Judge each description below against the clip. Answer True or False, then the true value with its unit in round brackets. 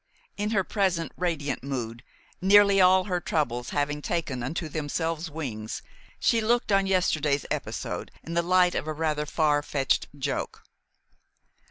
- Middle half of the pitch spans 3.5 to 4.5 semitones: True (4.2 semitones)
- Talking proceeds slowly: False (145 wpm)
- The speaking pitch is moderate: True (160 Hz)